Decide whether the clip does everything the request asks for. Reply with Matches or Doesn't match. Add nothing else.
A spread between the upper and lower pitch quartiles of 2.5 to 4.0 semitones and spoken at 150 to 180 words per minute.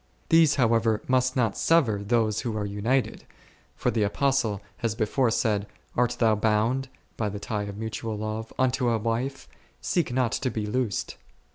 Matches